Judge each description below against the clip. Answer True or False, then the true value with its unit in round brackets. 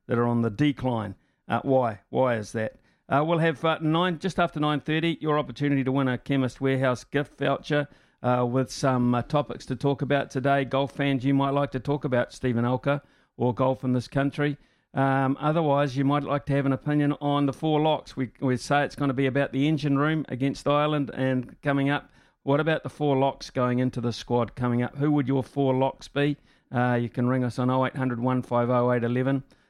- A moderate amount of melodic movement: False (2.3 semitones)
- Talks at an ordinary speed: False (225 wpm)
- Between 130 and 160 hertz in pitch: True (135 Hz)